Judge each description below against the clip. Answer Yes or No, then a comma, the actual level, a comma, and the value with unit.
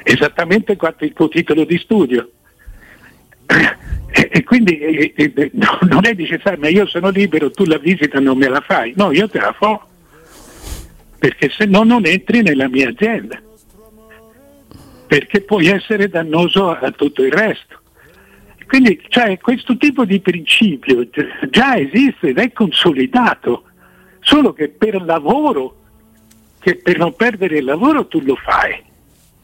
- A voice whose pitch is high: Yes, high, 195 Hz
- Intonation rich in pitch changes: Yes, wide, 6.0 semitones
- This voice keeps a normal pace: Yes, average, 145 wpm